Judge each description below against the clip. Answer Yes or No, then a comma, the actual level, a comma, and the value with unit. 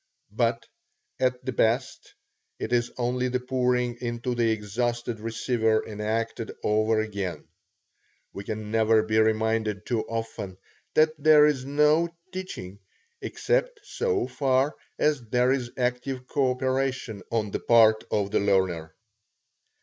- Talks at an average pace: No, slow, 125 wpm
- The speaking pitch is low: Yes, low, 120 Hz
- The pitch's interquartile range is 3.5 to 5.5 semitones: No, average, 2.9 semitones